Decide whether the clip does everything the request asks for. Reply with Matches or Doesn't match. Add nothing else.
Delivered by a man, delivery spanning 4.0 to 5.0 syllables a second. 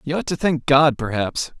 Matches